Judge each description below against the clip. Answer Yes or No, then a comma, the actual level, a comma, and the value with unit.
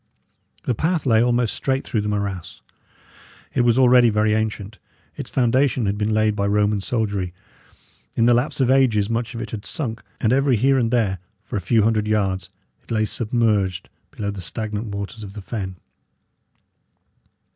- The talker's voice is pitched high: No, low, 110 Hz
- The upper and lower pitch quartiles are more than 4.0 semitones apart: No, average, 2.8 semitones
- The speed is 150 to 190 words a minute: Yes, average, 175 wpm